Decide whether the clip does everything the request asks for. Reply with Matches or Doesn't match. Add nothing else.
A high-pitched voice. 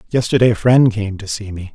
Doesn't match